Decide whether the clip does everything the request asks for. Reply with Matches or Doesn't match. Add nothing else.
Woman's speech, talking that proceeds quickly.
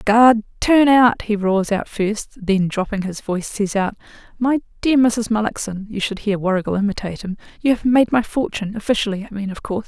Doesn't match